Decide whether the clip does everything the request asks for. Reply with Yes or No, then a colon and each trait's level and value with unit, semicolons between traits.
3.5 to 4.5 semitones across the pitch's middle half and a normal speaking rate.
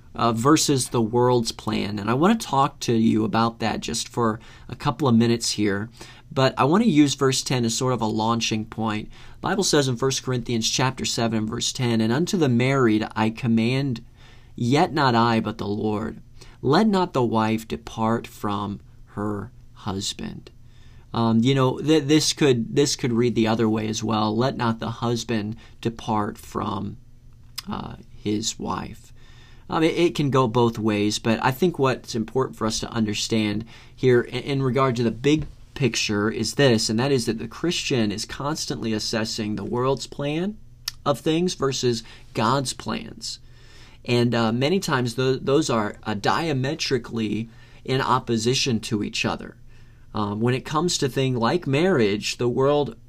No: average, 2.9 semitones; average, 175 wpm